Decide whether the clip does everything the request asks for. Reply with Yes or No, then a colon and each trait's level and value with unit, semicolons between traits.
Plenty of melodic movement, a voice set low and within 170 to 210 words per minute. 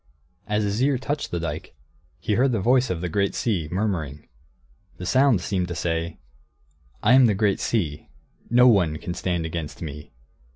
Yes: wide, 6.0 semitones; very low, 95 Hz; average, 175 wpm